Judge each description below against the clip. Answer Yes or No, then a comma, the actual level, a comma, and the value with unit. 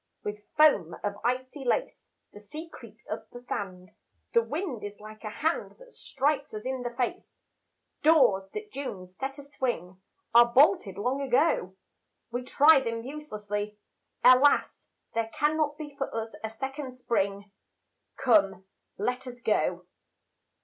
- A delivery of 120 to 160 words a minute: Yes, average, 145 wpm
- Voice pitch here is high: Yes, high, 245 Hz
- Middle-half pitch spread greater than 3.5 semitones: Yes, wide, 5.5 semitones